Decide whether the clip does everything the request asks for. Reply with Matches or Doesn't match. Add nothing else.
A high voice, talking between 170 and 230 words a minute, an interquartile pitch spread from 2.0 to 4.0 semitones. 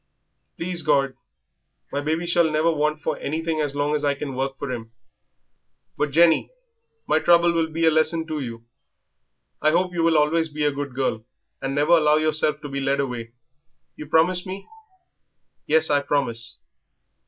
Doesn't match